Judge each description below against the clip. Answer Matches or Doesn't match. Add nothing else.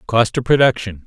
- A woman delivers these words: Doesn't match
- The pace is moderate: Matches